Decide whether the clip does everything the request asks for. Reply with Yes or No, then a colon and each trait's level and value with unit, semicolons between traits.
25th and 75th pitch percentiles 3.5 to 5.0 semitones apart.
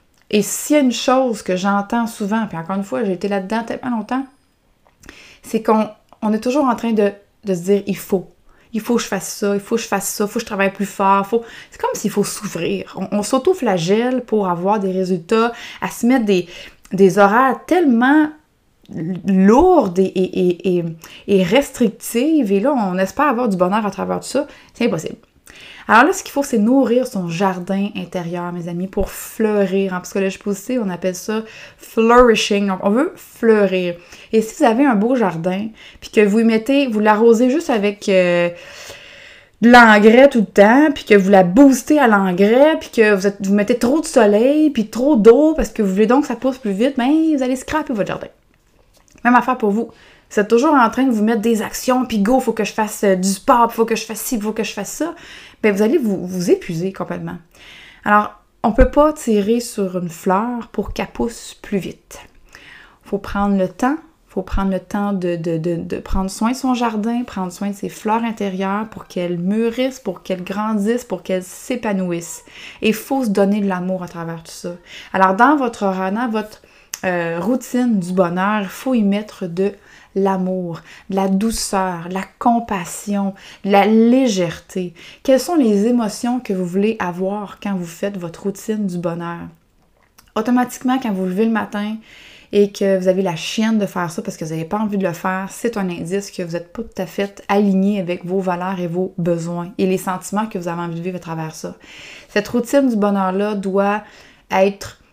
Yes: average, 3.8 semitones